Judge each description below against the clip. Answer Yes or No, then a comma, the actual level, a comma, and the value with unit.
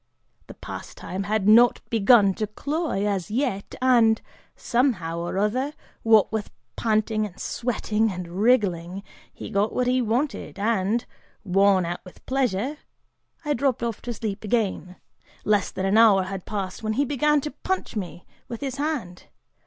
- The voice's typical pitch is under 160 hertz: No, high, 215 Hz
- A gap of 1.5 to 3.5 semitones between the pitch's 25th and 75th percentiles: No, average, 4.1 semitones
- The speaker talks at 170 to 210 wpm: No, average, 155 wpm